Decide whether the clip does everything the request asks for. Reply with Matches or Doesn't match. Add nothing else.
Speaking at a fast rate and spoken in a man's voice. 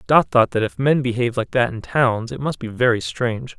Matches